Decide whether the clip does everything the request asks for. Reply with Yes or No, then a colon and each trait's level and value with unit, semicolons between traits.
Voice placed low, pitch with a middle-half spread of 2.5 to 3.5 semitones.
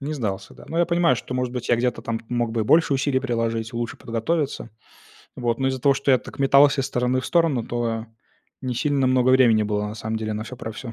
Yes: low, 125 Hz; average, 2.9 semitones